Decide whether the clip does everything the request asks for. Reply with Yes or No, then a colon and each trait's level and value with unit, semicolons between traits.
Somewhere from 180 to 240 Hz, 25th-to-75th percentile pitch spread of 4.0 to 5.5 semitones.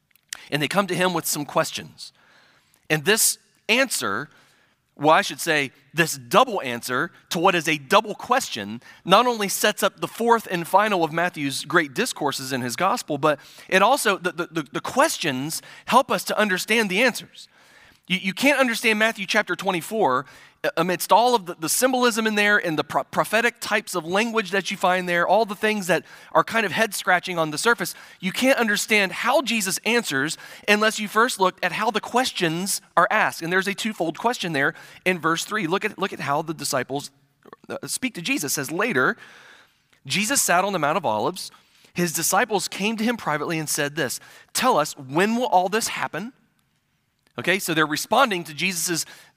Yes: medium, 185 Hz; average, 5.0 semitones